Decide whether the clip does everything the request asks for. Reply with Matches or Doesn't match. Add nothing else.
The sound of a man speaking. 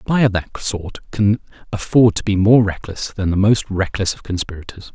Matches